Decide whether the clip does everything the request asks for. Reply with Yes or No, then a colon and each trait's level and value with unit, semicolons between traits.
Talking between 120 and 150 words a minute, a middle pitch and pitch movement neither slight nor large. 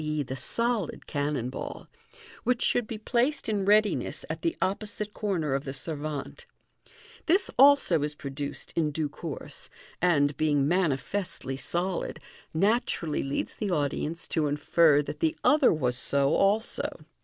No: average, 145 wpm; medium, 165 Hz; wide, 6.7 semitones